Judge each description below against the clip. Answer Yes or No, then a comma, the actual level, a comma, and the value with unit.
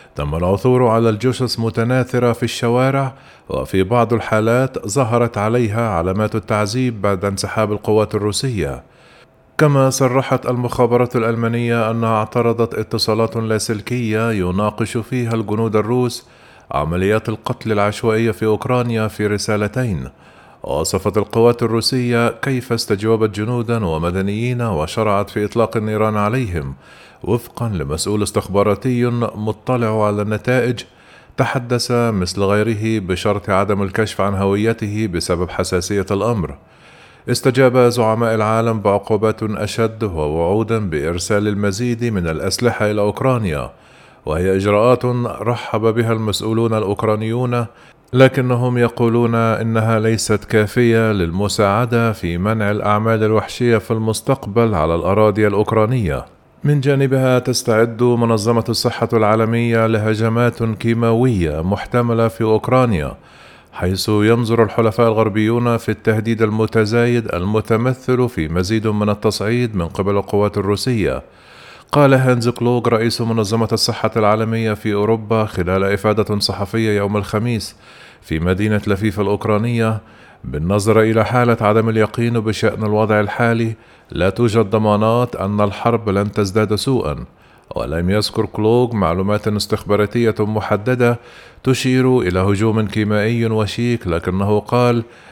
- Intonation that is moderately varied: No, narrow, 2.3 semitones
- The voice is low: Yes, low, 110 Hz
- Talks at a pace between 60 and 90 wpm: No, average, 110 wpm